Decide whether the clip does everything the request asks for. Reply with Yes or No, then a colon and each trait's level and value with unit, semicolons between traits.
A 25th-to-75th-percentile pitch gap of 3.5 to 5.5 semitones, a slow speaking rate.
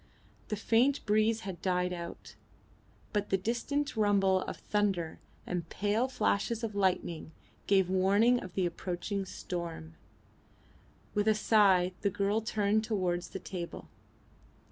No: average, 3.1 semitones; slow, 130 wpm